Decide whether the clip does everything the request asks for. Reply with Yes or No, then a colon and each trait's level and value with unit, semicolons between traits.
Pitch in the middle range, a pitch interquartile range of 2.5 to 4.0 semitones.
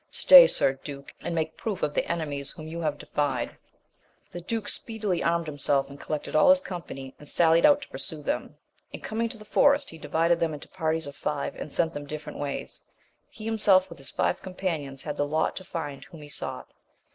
No: medium, 160 Hz; average, 4.4 semitones